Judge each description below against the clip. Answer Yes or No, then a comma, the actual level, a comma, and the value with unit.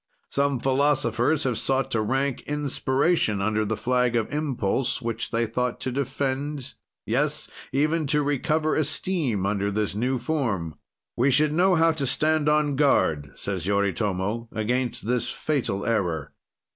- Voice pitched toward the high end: No, low, 130 Hz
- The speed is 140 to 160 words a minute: Yes, average, 145 wpm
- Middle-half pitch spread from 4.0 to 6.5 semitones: Yes, average, 5.2 semitones